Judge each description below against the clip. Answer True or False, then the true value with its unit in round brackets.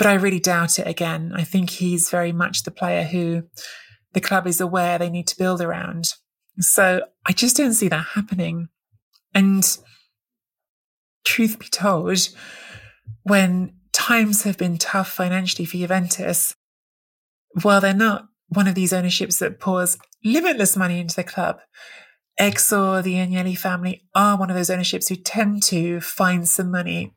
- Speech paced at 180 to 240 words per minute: False (155 wpm)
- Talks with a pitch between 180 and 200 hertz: True (185 Hz)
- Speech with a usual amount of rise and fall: False (2.1 semitones)